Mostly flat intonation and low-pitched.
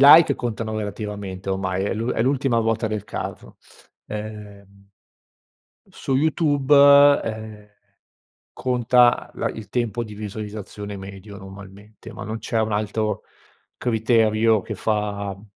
Yes: narrow, 2.0 semitones; low, 110 Hz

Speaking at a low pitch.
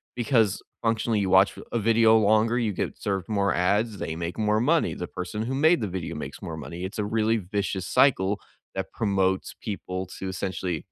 Yes: low, 100 Hz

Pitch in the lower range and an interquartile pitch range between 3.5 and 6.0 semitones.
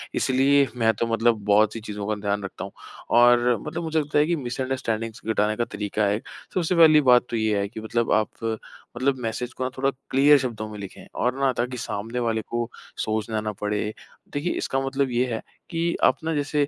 Yes: low, 120 Hz; average, 3.9 semitones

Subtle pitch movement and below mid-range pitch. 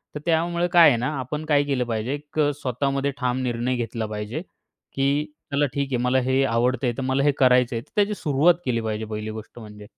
No: average, 3.6 semitones; low, 130 Hz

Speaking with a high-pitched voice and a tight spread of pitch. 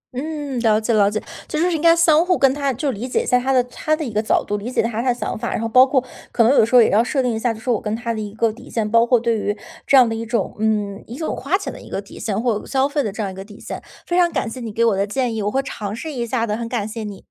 No: high, 235 Hz; average, 3.6 semitones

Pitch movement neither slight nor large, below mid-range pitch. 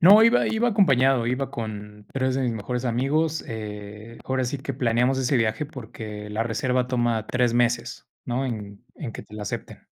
Yes: average, 3.3 semitones; low, 120 Hz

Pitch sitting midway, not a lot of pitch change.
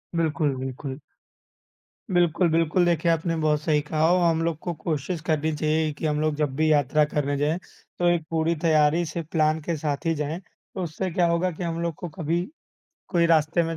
Yes: medium, 160 Hz; narrow, 1.9 semitones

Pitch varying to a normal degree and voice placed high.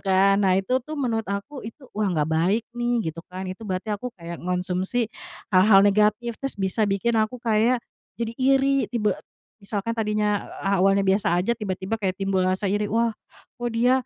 Yes: average, 3.5 semitones; high, 210 Hz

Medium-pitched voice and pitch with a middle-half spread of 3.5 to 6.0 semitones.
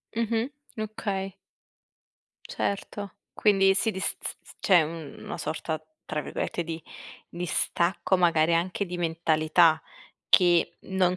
No: medium, 175 Hz; average, 2.8 semitones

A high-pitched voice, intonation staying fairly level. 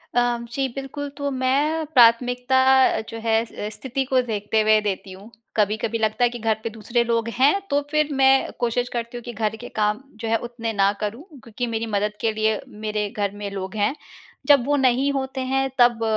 No: high, 235 Hz; average, 3.5 semitones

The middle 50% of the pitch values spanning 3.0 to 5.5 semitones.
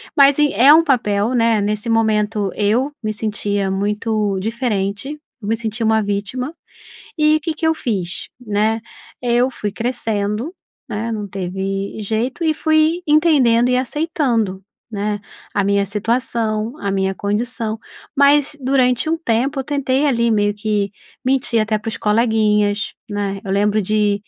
Yes: average, 3.9 semitones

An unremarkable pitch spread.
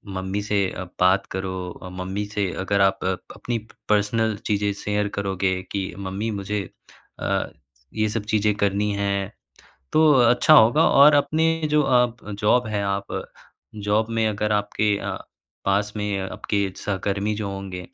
No: narrow, 1.7 semitones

